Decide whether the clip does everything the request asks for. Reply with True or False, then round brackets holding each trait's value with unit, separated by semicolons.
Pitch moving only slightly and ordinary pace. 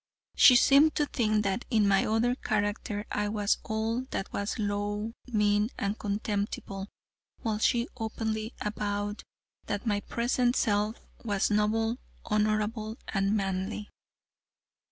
False (1.5 semitones; 125 wpm)